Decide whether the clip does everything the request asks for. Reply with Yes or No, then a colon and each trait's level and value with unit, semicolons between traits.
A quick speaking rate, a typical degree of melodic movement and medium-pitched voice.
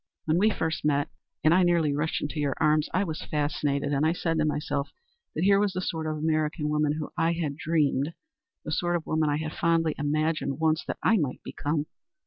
No: fast, 220 wpm; narrow, 1.9 semitones; medium, 155 Hz